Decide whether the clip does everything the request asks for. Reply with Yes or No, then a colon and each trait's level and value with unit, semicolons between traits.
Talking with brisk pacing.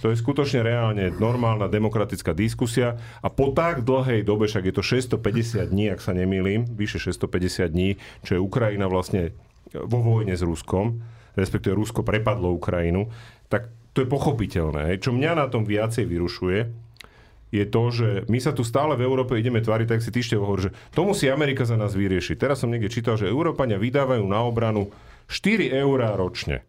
Yes: fast, 180 wpm